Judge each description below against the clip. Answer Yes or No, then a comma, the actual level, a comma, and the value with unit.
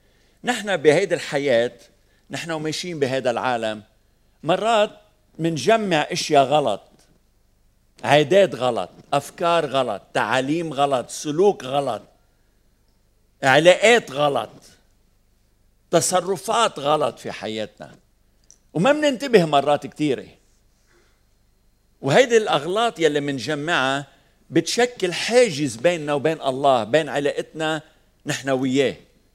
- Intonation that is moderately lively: No, wide, 6.5 semitones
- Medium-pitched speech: Yes, medium, 145 Hz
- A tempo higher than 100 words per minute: No, average, 85 wpm